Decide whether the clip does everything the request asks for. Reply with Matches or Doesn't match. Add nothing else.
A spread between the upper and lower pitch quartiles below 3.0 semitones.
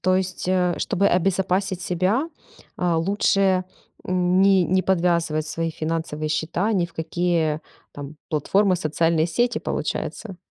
Matches